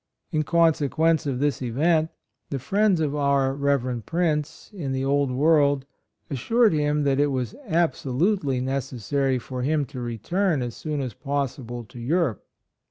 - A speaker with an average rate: Yes, average, 155 wpm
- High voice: No, medium, 140 Hz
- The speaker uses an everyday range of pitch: Yes, average, 3.3 semitones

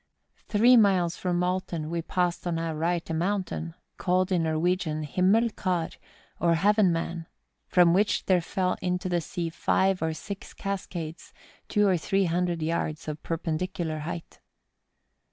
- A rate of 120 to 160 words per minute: Yes, average, 150 wpm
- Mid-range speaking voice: Yes, medium, 175 Hz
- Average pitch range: No, narrow, 2.2 semitones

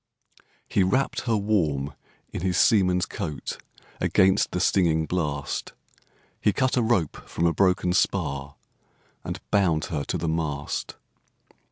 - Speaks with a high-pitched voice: No, very low, 90 Hz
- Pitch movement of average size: Yes, average, 4.3 semitones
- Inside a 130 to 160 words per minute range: Yes, slow, 135 wpm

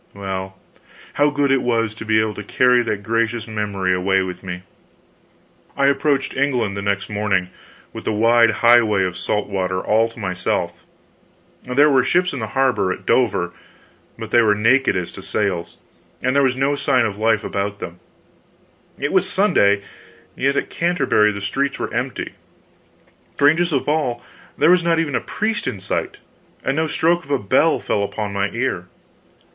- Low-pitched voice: Yes, low, 115 Hz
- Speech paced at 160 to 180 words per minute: Yes, average, 175 wpm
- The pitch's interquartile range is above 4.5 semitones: Yes, wide, 5.4 semitones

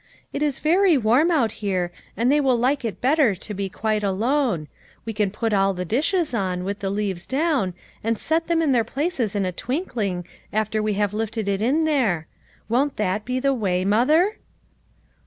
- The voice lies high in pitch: Yes, high, 225 Hz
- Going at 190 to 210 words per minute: Yes, average, 195 wpm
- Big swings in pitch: Yes, wide, 5.9 semitones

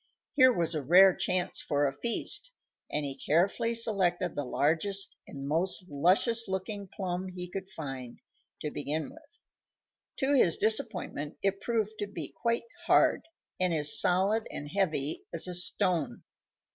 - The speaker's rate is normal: Yes, average, 150 wpm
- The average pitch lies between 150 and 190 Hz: Yes, medium, 185 Hz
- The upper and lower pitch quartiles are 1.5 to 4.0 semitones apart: No, average, 5.1 semitones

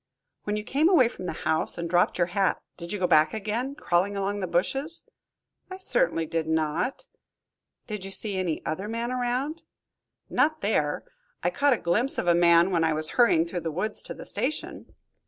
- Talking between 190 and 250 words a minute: Yes, average, 200 wpm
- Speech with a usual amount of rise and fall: No, wide, 6.3 semitones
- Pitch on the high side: Yes, high, 195 Hz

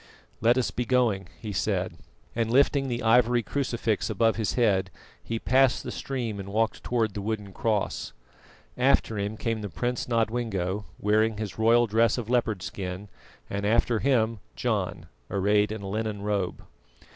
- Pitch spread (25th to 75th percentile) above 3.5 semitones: No, average, 2.7 semitones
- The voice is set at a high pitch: No, low, 110 Hz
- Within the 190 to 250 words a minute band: No, average, 160 wpm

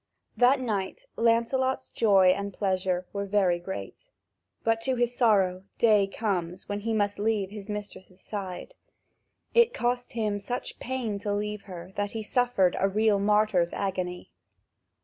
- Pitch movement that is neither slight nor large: Yes, average, 3.0 semitones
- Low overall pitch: No, high, 205 Hz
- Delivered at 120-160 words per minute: Yes, average, 150 wpm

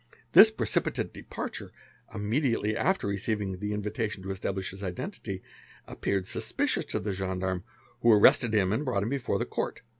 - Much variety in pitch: No, average, 2.8 semitones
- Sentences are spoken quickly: No, average, 160 wpm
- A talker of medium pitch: No, low, 105 Hz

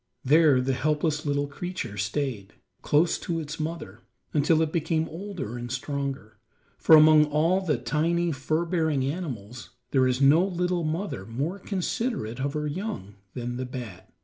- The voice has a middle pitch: Yes, medium, 150 Hz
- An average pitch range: Yes, average, 4.5 semitones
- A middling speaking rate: Yes, average, 155 wpm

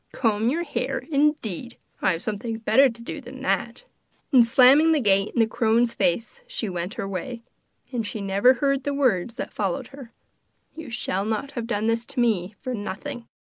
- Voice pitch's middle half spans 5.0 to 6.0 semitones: No, average, 4.4 semitones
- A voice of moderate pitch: No, high, 230 Hz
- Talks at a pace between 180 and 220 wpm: Yes, average, 190 wpm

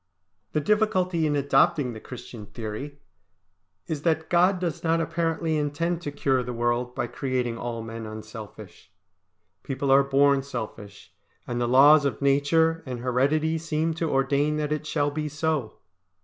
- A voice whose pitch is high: No, medium, 140 Hz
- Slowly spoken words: No, average, 155 wpm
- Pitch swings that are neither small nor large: Yes, average, 4.5 semitones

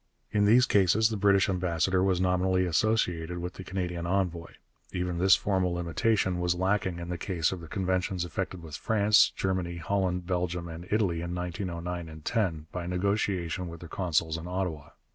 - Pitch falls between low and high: No, very low, 90 Hz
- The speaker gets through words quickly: No, average, 170 wpm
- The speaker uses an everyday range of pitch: No, narrow, 1.9 semitones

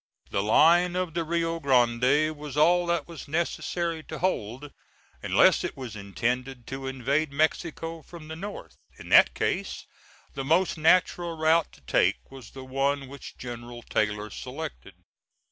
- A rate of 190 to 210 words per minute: No, average, 150 wpm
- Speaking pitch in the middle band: Yes, medium, 145 Hz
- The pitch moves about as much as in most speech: Yes, average, 4.8 semitones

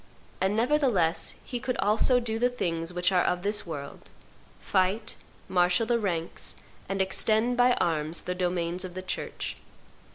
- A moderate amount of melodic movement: Yes, average, 4.5 semitones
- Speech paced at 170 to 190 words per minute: No, average, 155 wpm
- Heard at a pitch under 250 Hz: Yes, high, 190 Hz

